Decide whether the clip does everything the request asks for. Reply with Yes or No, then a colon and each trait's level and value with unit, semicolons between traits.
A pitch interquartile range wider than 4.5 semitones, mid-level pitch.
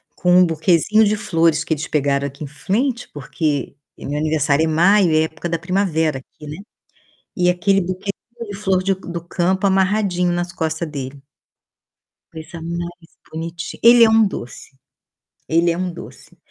No: average, 3.4 semitones; medium, 170 Hz